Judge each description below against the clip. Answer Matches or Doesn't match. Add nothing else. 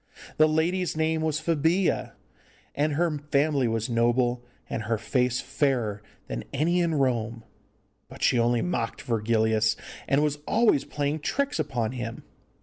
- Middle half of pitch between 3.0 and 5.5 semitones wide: Matches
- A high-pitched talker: Doesn't match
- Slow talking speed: Doesn't match